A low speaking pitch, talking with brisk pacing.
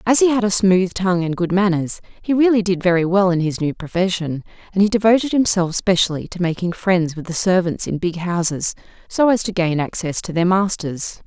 No: medium, 185 Hz; fast, 215 wpm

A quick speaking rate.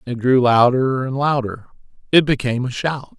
No: average, 150 wpm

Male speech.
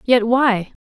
No: female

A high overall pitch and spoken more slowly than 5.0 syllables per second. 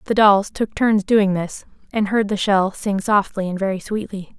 Yes: high, 200 Hz; 4.6 syllables/s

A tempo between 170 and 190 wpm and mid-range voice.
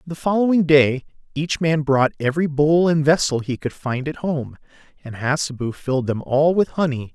Yes: average, 185 wpm; medium, 145 Hz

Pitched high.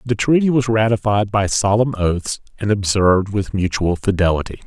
No: low, 105 Hz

